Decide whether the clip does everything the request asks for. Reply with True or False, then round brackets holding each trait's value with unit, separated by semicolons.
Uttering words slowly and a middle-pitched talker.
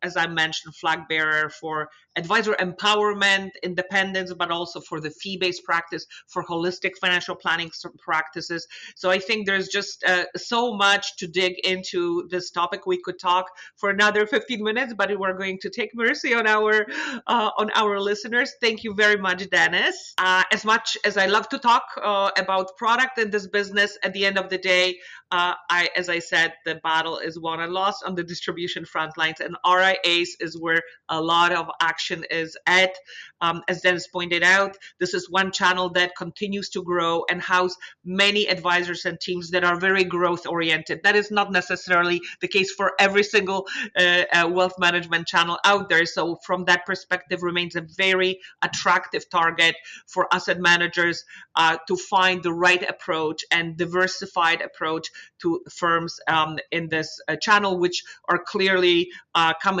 False (180 wpm; 180 Hz)